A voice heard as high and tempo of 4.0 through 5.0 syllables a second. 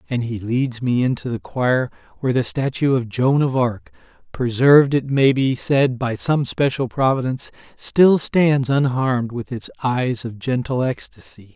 No: low, 130 Hz; 4.5 syllables/s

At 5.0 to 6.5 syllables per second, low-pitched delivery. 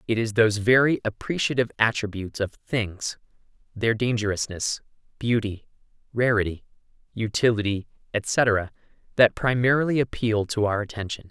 Yes: 5.2 syllables/s; low, 110 Hz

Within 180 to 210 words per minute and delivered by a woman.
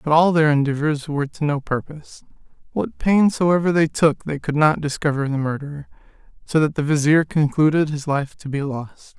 No: average, 190 wpm; male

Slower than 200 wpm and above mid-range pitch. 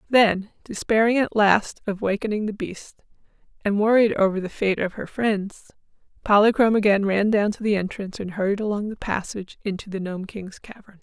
Yes: average, 180 wpm; high, 205 Hz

